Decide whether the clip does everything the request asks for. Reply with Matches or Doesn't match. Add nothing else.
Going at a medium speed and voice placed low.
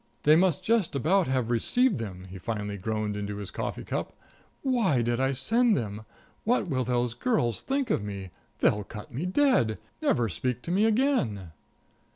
Matches